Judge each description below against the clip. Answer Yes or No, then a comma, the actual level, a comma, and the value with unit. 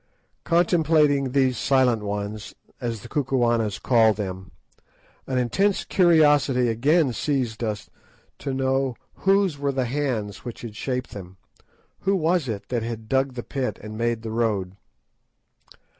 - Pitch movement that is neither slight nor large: Yes, average, 4.3 semitones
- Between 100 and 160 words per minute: Yes, average, 140 wpm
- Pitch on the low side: Yes, low, 125 Hz